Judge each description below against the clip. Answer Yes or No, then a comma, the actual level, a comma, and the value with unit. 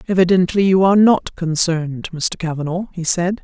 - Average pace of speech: Yes, average, 155 wpm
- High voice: No, medium, 175 Hz